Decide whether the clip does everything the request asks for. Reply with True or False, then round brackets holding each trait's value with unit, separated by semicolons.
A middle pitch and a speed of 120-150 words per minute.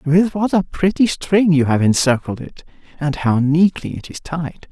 False (160 Hz; 180 wpm)